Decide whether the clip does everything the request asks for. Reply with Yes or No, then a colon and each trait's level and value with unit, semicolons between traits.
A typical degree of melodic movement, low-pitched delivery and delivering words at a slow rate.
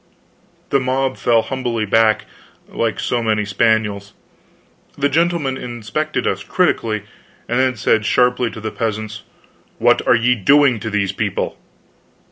Yes: average, 3.3 semitones; low, 115 Hz; slow, 130 wpm